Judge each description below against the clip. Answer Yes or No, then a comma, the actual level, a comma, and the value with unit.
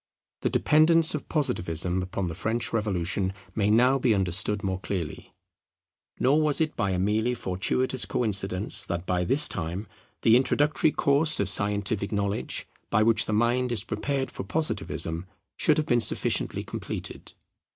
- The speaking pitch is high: No, low, 105 Hz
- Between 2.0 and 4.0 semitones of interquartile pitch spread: No, wide, 5.5 semitones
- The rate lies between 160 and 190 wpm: No, average, 150 wpm